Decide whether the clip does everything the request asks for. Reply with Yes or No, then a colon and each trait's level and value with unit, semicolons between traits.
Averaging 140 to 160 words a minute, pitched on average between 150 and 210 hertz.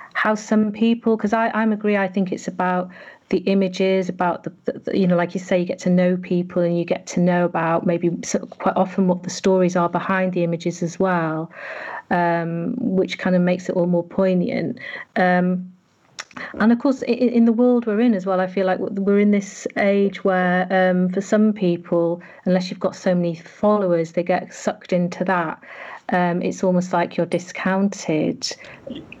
No: average, 195 wpm; medium, 185 Hz